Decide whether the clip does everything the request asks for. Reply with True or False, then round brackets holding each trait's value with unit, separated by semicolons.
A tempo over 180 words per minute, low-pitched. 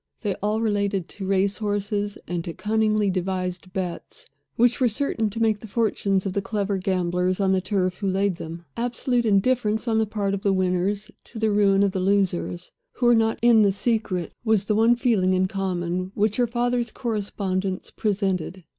False (190 wpm; 200 Hz)